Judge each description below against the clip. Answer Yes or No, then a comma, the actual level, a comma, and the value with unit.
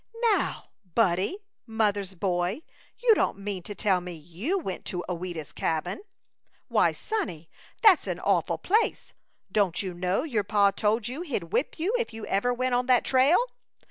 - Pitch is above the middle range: Yes, high, 205 Hz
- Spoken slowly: No, average, 165 wpm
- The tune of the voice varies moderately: No, wide, 6.0 semitones